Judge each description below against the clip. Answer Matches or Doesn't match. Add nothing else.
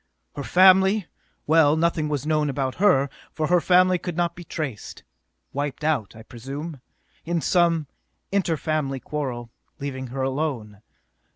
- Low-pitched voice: Doesn't match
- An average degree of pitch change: Matches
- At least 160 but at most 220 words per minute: Doesn't match